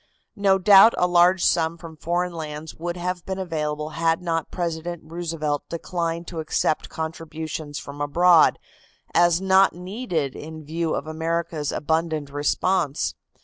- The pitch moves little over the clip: Yes, narrow, 2.0 semitones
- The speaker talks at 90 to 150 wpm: Yes, average, 140 wpm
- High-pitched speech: No, medium, 165 Hz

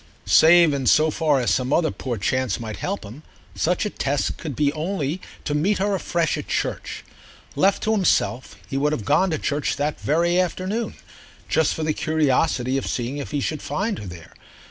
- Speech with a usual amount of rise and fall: Yes, average, 4.4 semitones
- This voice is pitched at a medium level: Yes, medium, 150 Hz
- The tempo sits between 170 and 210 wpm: Yes, average, 200 wpm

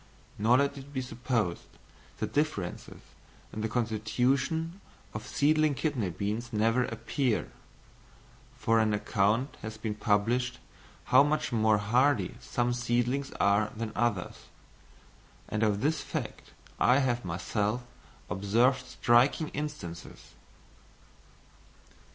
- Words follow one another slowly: Yes, slow, 110 wpm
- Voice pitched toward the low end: Yes, low, 120 Hz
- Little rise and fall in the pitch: No, average, 3.9 semitones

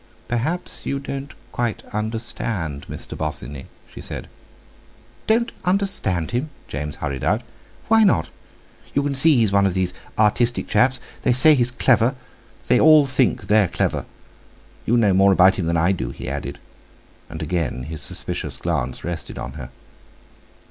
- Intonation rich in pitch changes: Yes, wide, 7.8 semitones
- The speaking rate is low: No, average, 150 wpm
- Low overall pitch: Yes, low, 110 Hz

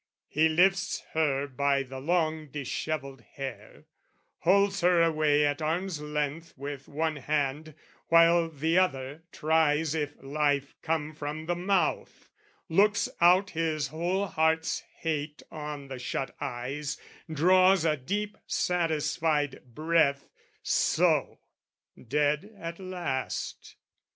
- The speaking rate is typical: No, slow, 115 wpm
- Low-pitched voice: No, medium, 155 Hz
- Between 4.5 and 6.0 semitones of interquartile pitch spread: No, narrow, 2.6 semitones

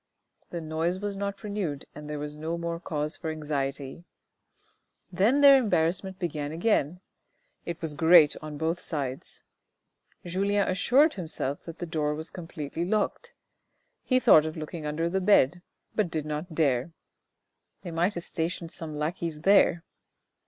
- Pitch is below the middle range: No, medium, 165 Hz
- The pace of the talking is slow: No, average, 160 wpm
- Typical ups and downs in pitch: Yes, average, 3.4 semitones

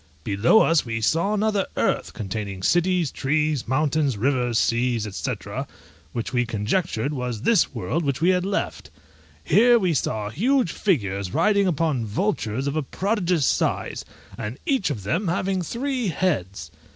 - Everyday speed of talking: Yes, average, 150 wpm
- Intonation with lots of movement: Yes, wide, 8.5 semitones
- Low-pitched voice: No, medium, 150 Hz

